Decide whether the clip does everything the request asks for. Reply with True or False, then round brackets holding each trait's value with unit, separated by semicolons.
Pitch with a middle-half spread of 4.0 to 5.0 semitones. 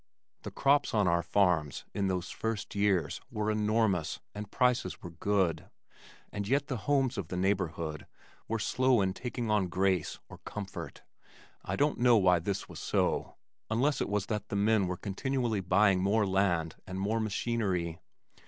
False (3.5 semitones)